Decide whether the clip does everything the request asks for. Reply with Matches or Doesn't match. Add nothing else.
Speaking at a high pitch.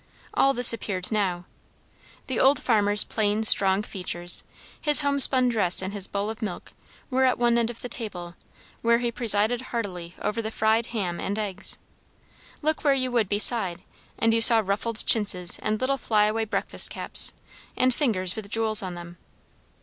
Matches